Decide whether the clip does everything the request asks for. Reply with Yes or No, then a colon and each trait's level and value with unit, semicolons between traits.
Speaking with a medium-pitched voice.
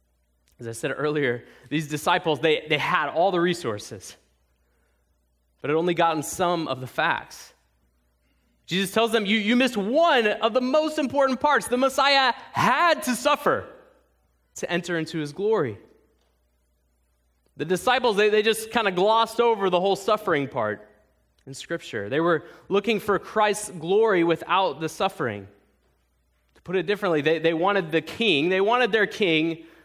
Yes: medium, 170 Hz